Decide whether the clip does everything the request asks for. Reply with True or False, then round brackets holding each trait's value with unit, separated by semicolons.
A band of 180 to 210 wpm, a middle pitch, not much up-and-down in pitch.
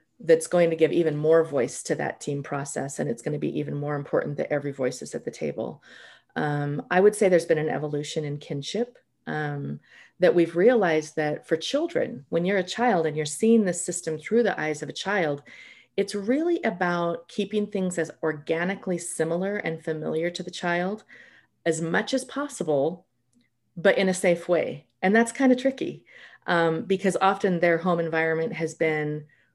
False (190 wpm; 170 Hz; 4.4 semitones)